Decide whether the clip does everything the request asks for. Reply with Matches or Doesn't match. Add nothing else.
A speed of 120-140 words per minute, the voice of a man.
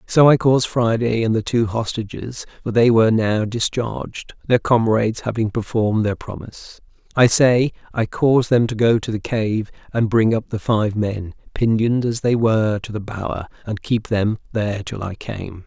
Doesn't match